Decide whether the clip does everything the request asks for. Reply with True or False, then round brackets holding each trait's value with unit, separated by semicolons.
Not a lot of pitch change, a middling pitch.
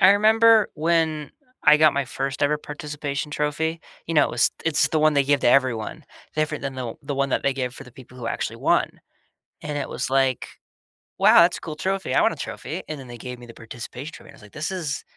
False (3.1 semitones; 145 Hz)